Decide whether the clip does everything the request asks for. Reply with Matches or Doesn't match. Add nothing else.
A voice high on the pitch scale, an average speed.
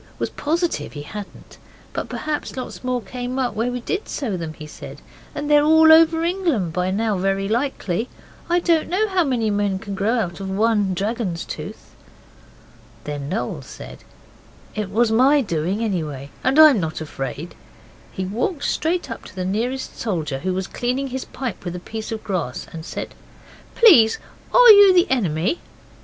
Matches